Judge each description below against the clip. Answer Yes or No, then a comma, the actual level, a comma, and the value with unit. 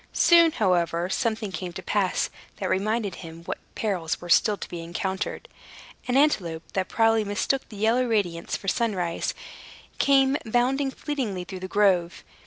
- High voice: Yes, high, 205 Hz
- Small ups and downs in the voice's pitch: No, average, 5.0 semitones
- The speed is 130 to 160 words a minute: Yes, average, 155 wpm